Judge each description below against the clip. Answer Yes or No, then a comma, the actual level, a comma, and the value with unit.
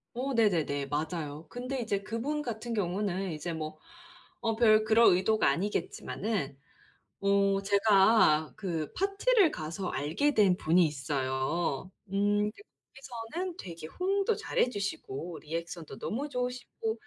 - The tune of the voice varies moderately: No, wide, 6.3 semitones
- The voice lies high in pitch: Yes, high, 200 Hz